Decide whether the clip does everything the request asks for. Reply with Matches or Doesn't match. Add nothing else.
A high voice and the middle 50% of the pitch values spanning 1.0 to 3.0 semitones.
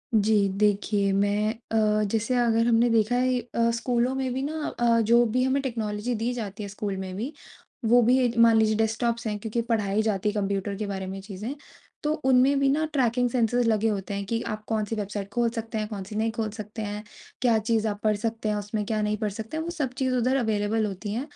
Matches